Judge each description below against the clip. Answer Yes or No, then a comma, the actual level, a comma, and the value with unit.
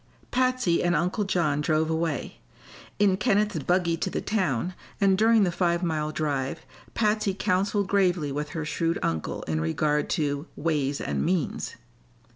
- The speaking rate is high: No, average, 150 wpm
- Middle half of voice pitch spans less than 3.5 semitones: No, average, 4.5 semitones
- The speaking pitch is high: No, medium, 170 Hz